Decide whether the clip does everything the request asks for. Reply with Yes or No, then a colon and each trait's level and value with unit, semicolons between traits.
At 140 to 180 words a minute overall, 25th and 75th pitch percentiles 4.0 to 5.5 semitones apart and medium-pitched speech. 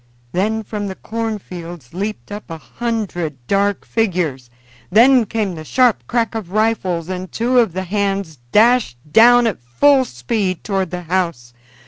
No: average, 150 wpm; average, 4.4 semitones; high, 200 Hz